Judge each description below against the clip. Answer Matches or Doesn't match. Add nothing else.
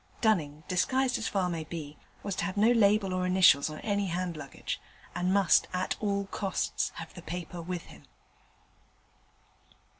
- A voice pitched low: Doesn't match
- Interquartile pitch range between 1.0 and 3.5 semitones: Matches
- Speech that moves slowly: Doesn't match